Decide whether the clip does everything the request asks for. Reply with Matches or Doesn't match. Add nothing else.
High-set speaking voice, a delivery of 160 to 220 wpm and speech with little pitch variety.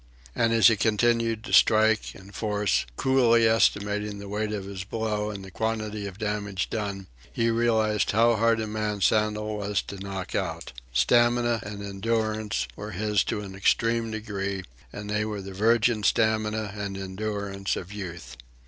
Doesn't match